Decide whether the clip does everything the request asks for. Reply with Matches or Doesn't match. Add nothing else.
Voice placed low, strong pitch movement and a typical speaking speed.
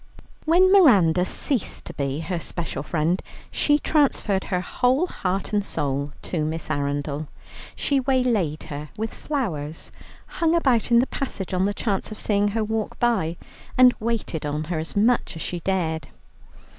Doesn't match